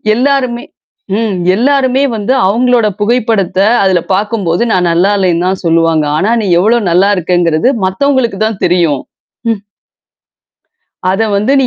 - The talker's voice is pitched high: Yes, high, 200 Hz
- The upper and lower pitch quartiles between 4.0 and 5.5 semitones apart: Yes, average, 5.1 semitones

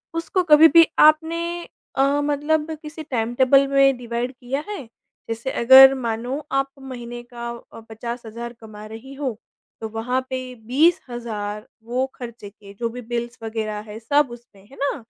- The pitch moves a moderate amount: Yes, average, 3.2 semitones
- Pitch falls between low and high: No, high, 245 Hz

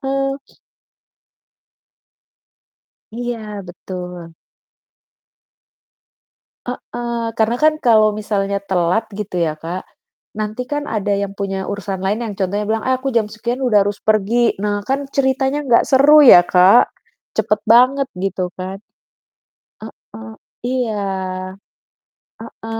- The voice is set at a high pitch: Yes, high, 215 Hz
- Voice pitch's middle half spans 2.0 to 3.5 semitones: No, average, 4.0 semitones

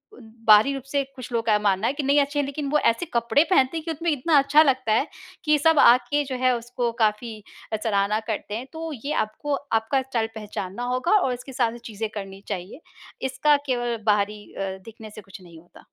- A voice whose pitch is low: No, high, 240 Hz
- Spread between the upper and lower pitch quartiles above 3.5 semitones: Yes, average, 4.6 semitones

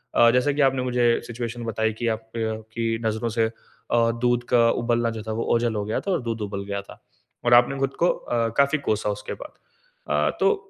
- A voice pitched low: Yes, low, 115 Hz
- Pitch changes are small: Yes, narrow, 1.9 semitones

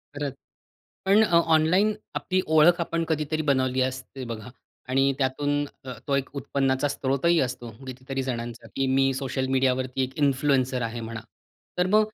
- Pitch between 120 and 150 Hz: Yes, low, 135 Hz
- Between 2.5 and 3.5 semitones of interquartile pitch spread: Yes, average, 2.8 semitones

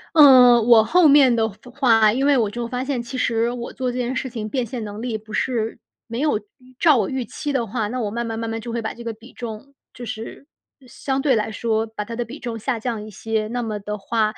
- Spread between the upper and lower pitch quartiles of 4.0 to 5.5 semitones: No, narrow, 2.5 semitones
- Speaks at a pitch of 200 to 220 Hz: No, high, 235 Hz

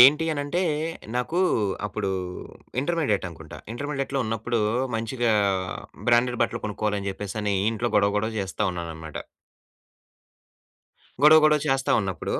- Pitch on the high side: No, low, 115 Hz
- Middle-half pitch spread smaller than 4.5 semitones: No, average, 5.1 semitones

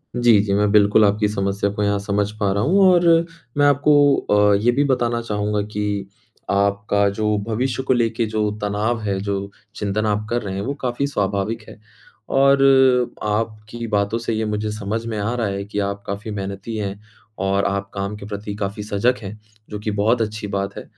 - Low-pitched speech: Yes, low, 105 Hz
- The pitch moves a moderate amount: No, narrow, 2.2 semitones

